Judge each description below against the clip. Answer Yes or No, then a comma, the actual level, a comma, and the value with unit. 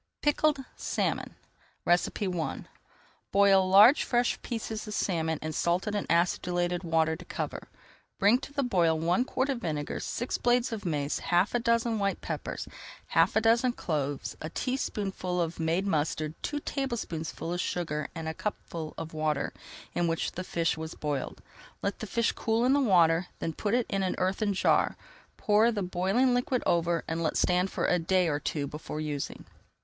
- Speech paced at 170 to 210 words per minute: Yes, average, 175 wpm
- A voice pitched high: No, medium, 180 Hz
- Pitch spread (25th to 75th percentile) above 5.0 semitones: Yes, wide, 5.6 semitones